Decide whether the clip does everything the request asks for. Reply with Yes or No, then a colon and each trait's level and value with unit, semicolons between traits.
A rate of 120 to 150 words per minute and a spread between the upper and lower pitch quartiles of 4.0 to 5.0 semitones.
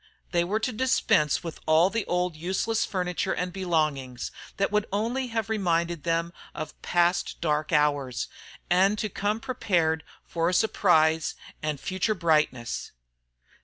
Yes: average, 140 wpm; average, 4.3 semitones